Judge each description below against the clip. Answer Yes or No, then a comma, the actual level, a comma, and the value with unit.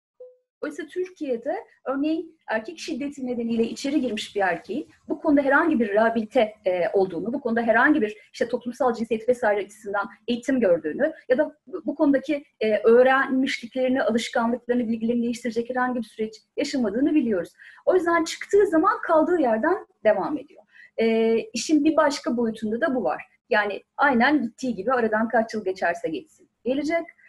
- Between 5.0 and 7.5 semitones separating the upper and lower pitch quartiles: Yes, average, 5.3 semitones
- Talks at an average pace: No, fast, 145 wpm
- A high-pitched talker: Yes, very high, 255 Hz